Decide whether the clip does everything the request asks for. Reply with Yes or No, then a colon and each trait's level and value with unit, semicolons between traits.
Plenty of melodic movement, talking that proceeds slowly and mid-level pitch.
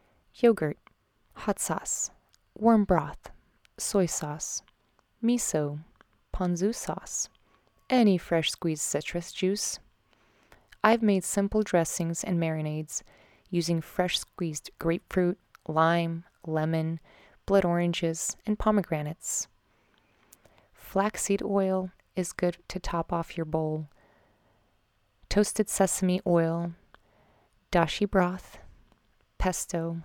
No: average, 3.6 semitones; slow, 90 wpm; medium, 175 Hz